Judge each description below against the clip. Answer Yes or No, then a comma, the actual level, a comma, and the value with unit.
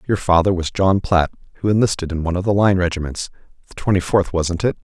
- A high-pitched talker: No, very low, 90 Hz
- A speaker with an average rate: No, fast, 210 wpm